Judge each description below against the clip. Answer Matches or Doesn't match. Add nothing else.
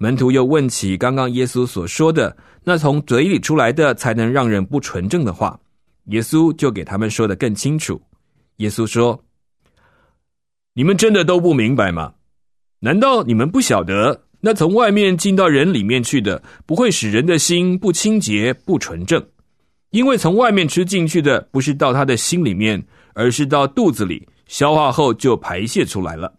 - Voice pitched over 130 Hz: Matches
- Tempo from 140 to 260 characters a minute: Matches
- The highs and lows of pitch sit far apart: Matches